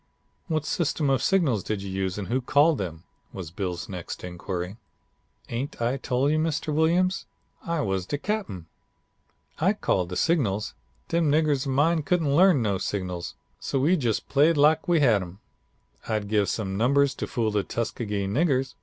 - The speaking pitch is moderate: No, low, 130 Hz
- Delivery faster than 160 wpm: Yes, average, 170 wpm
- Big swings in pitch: Yes, wide, 7.9 semitones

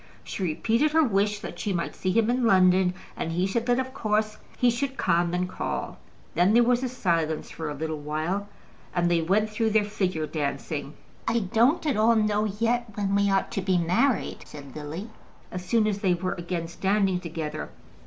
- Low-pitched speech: No, high, 195 Hz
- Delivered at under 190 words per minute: No, average, 195 wpm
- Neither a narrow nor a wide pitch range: Yes, average, 4.5 semitones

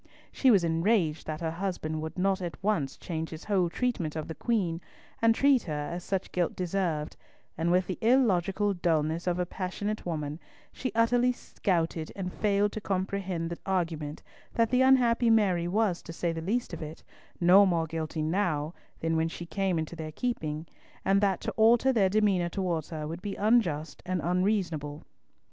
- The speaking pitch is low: No, medium, 180 Hz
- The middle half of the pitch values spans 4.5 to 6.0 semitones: No, average, 4.1 semitones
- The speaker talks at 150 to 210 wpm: Yes, average, 180 wpm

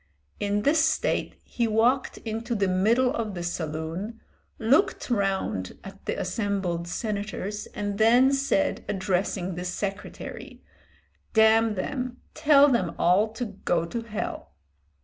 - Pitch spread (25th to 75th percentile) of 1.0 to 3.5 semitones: No, average, 3.9 semitones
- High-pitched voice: Yes, high, 210 Hz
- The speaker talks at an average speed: No, slow, 130 wpm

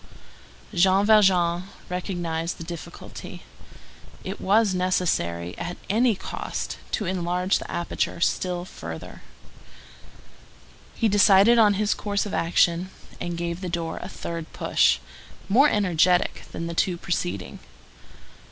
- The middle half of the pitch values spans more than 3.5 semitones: No, average, 2.7 semitones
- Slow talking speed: Yes, slow, 120 wpm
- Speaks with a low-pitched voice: No, medium, 180 Hz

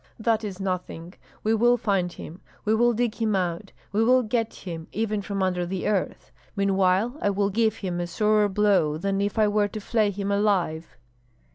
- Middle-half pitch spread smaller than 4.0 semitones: Yes, average, 2.8 semitones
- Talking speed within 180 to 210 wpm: Yes, average, 190 wpm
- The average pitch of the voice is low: No, high, 200 Hz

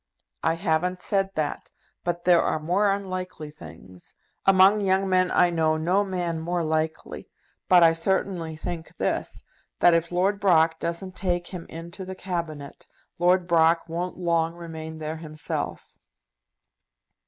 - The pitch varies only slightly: Yes, narrow, 2.3 semitones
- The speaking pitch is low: No, medium, 170 Hz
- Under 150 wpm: Yes, average, 140 wpm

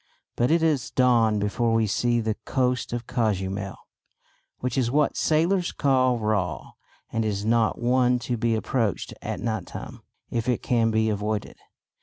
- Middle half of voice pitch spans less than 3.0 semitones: Yes, narrow, 2.6 semitones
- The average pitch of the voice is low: Yes, low, 115 Hz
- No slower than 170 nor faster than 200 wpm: No, average, 160 wpm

